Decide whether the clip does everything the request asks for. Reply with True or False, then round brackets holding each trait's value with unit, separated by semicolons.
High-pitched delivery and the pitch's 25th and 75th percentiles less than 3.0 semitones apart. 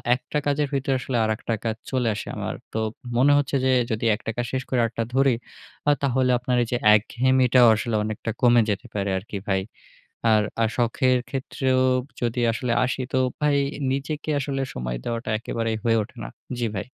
False (125 Hz; 2.5 semitones)